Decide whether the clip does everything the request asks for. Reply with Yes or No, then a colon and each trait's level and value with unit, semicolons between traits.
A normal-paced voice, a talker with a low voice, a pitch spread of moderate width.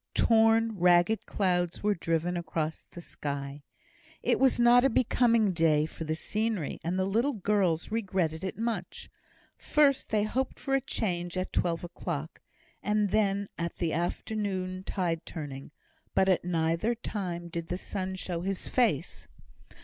No: average, 150 wpm; medium, 185 Hz; average, 4.4 semitones